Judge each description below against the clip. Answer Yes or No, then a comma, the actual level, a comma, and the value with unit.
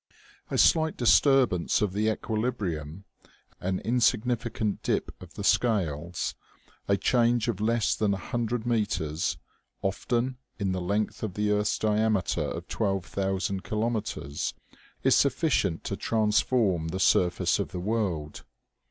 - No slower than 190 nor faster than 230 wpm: No, slow, 135 wpm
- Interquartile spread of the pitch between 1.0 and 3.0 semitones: No, average, 3.8 semitones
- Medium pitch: No, low, 105 Hz